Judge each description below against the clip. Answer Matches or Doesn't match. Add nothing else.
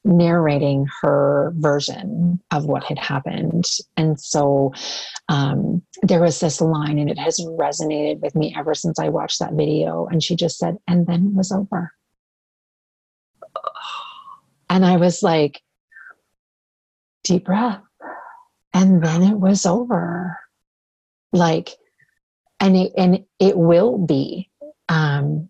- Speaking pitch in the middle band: Matches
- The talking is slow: Matches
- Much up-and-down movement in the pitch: Doesn't match